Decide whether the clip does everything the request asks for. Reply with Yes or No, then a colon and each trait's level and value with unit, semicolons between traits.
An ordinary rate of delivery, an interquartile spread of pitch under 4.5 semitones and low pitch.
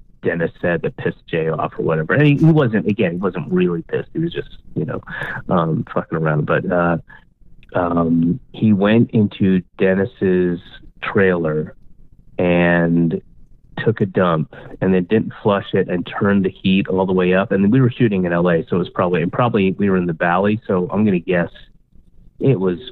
Yes: average, 190 wpm; average, 3.3 semitones; very low, 95 Hz